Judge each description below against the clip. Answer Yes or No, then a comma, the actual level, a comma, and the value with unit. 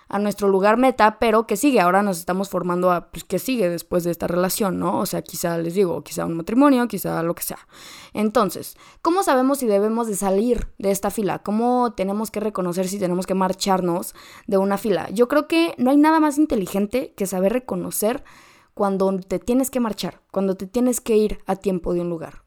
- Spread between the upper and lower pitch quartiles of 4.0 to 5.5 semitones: Yes, average, 4.4 semitones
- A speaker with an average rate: No, fast, 210 wpm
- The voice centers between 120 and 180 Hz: No, high, 200 Hz